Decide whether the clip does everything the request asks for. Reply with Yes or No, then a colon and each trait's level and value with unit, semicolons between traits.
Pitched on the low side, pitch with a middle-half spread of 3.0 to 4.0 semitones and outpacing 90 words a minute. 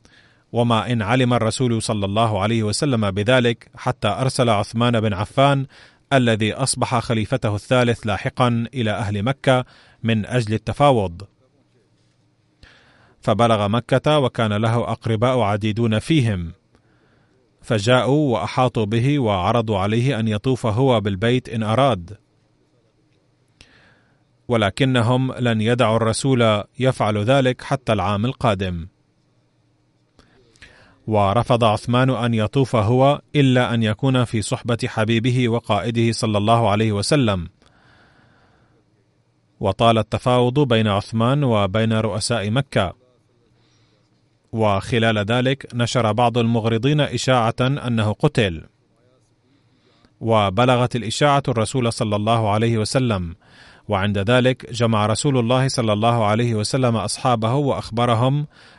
No: low, 115 Hz; narrow, 2.6 semitones; average, 105 wpm